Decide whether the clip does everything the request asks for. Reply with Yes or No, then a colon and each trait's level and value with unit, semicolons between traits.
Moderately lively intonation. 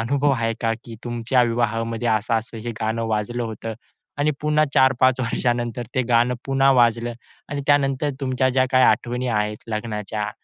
No: narrow, 2.3 semitones